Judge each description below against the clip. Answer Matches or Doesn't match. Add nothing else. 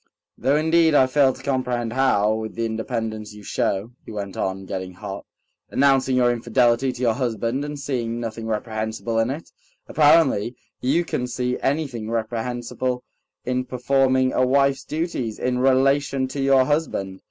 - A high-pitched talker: Doesn't match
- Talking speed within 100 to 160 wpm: Matches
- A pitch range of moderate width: Matches